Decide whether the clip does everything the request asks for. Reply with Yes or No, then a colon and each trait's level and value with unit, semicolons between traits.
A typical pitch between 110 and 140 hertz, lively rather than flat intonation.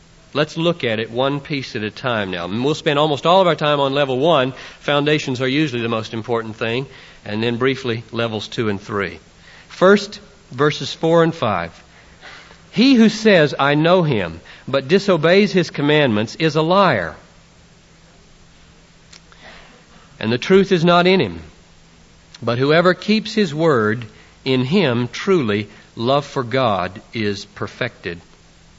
Yes: low, 135 Hz; wide, 7.0 semitones